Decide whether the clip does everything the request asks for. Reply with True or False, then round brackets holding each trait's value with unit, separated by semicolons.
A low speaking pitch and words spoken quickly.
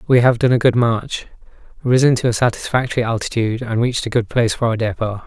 True (120 Hz; 215 wpm)